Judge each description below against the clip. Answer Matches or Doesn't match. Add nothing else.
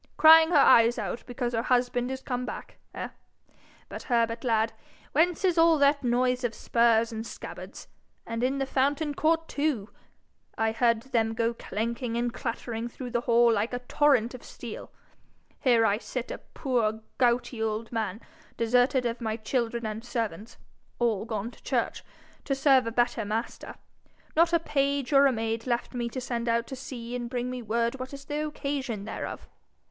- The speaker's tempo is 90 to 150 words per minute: Doesn't match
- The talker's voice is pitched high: Matches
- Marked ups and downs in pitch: Doesn't match